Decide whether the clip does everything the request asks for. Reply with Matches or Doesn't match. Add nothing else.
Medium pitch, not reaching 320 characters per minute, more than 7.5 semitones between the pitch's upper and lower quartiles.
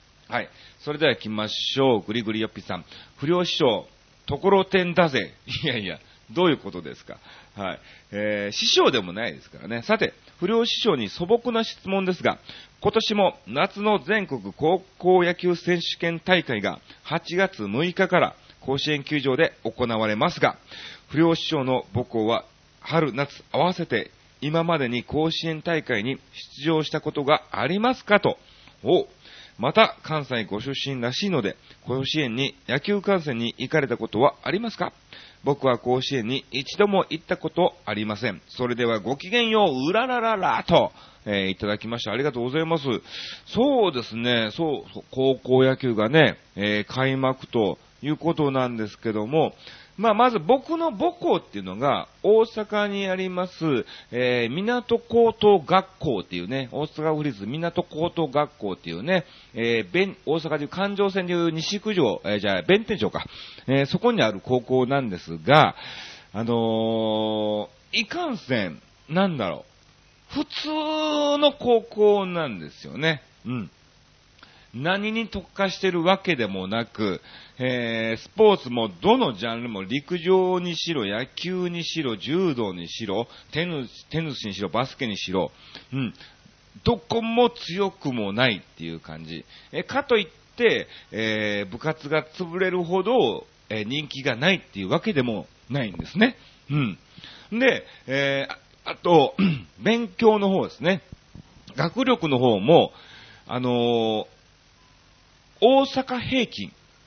Matches